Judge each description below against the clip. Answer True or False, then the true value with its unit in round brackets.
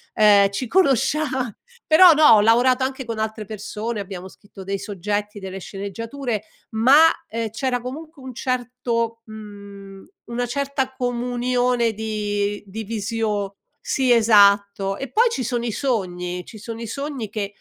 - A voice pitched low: False (225 Hz)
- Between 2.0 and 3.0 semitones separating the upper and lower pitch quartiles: False (3.6 semitones)